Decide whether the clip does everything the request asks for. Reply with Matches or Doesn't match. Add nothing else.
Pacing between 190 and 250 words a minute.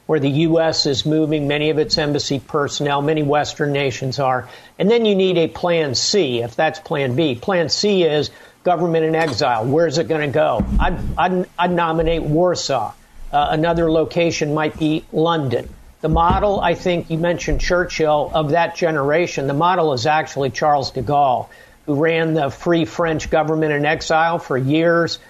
Doesn't match